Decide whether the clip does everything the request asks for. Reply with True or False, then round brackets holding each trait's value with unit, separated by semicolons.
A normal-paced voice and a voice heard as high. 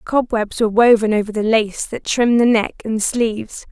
True (195 wpm; 225 Hz)